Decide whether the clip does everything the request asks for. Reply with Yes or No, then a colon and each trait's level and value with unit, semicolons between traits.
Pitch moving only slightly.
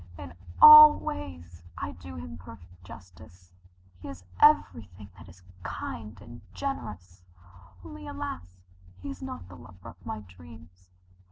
Yes: narrow, 2.3 semitones